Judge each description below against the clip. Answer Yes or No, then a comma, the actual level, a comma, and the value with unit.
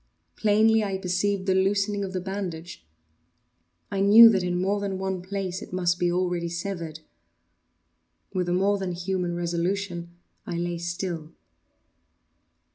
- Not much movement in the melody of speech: Yes, narrow, 2.3 semitones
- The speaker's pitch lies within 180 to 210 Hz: Yes, medium, 185 Hz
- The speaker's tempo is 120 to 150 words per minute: Yes, average, 140 wpm